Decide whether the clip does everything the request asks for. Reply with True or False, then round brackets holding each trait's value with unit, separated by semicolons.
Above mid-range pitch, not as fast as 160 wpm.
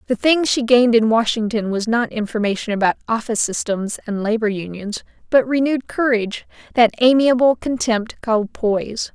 True (230 Hz; 150 wpm)